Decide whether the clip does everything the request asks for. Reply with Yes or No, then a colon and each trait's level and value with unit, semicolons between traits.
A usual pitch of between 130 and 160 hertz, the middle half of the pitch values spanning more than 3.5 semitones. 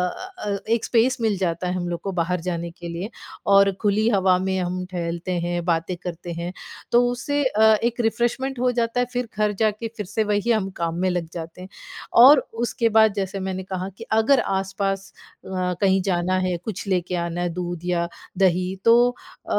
No: high, 190 Hz; average, 3.9 semitones